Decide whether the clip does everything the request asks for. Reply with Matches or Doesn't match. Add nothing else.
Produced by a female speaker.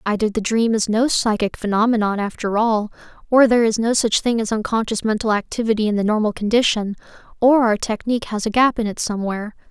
Matches